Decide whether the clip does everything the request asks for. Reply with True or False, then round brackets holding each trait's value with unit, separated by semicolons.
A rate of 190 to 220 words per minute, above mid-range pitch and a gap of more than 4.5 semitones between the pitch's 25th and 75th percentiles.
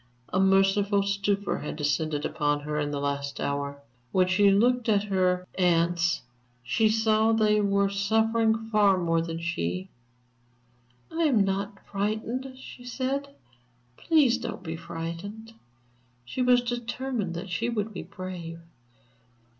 False (140 wpm; 200 Hz; 4.9 semitones)